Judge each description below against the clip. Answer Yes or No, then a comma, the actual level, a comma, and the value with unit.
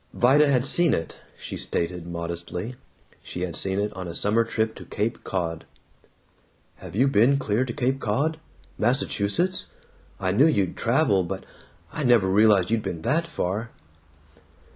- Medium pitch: No, low, 110 Hz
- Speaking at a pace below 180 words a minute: Yes, average, 155 wpm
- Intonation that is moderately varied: No, wide, 5.8 semitones